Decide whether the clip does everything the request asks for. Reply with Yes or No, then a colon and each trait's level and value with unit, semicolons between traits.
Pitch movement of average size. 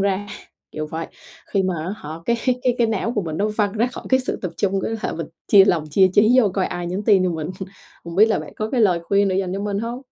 Yes: average, 3.5 semitones